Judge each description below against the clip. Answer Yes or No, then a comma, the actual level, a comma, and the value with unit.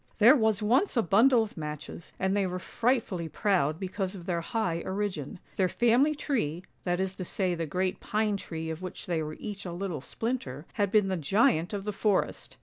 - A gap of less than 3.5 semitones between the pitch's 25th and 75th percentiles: No, average, 4.0 semitones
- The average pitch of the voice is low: No, high, 190 Hz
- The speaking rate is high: Yes, fast, 215 wpm